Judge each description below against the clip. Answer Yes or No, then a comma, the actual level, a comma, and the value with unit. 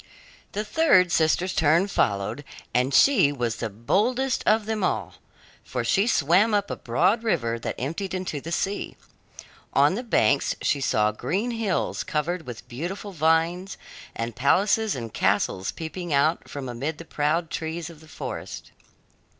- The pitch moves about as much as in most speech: No, wide, 6.3 semitones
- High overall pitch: No, medium, 160 Hz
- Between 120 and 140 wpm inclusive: No, average, 155 wpm